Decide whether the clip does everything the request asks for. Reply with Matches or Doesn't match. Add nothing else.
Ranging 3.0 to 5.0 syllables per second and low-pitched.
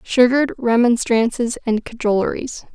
Doesn't match